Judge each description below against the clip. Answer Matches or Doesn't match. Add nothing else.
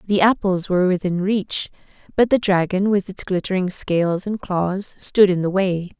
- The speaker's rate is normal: Matches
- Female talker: Matches